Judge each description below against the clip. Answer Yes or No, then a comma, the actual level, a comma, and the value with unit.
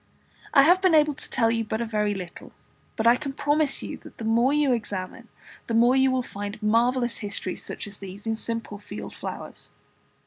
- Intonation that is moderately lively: Yes, average, 4.0 semitones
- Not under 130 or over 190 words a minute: No, average, 200 wpm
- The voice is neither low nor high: No, high, 230 Hz